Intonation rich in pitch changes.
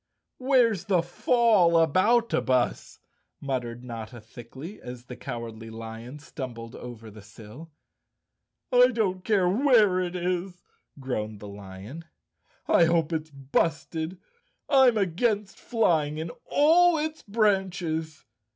Yes: wide, 9.0 semitones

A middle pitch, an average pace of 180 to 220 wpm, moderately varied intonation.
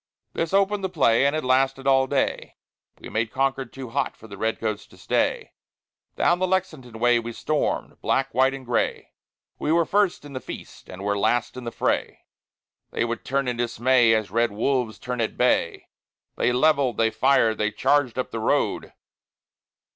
No: low, 125 Hz; average, 185 wpm; average, 3.2 semitones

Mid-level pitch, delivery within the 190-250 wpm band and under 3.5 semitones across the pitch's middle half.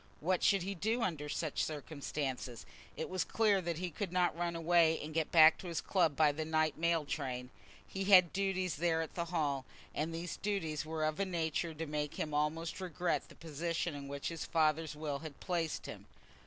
Yes: medium, 160 Hz; fast, 205 wpm; narrow, 2.5 semitones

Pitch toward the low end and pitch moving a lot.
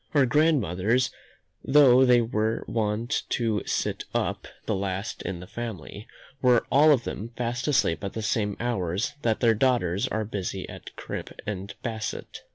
No: low, 110 Hz; average, 3.7 semitones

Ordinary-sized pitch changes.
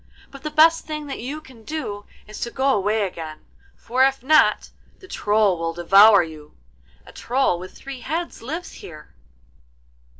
No: wide, 7.0 semitones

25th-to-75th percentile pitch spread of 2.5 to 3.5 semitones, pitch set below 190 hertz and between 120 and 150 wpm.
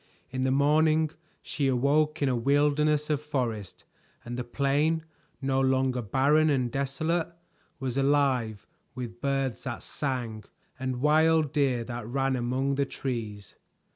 Yes: average, 3.0 semitones; low, 135 Hz; average, 140 wpm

